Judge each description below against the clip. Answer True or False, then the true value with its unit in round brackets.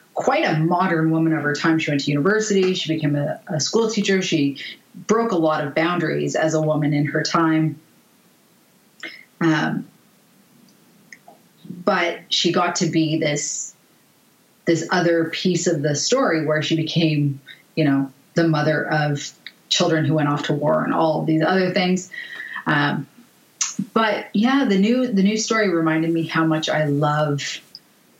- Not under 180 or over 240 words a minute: False (160 wpm)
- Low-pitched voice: False (165 Hz)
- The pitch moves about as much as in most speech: True (4.2 semitones)